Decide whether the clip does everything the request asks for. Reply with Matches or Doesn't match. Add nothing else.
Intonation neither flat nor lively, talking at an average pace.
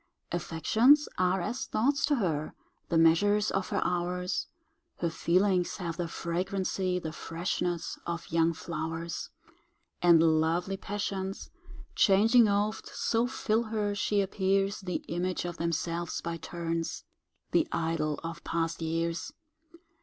Doesn't match